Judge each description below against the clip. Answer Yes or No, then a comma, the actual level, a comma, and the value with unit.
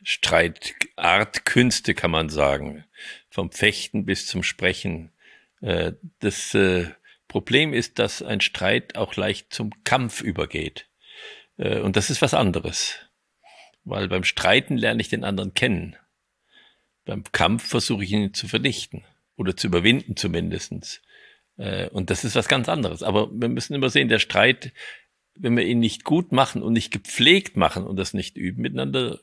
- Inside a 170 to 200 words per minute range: No, average, 150 wpm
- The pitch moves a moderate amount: No, wide, 6.5 semitones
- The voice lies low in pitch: Yes, low, 100 Hz